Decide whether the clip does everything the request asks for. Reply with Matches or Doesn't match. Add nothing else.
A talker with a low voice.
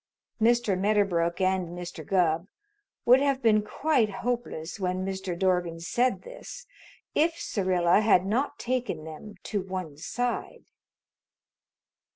Doesn't match